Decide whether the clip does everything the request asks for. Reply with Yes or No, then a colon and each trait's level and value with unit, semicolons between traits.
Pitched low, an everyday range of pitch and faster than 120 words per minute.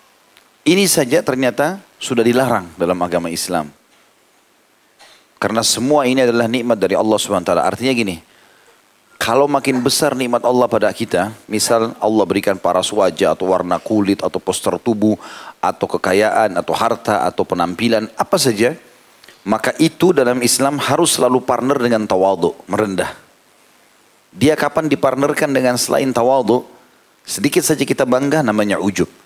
Yes: low, 125 Hz; average, 4.4 semitones; average, 135 wpm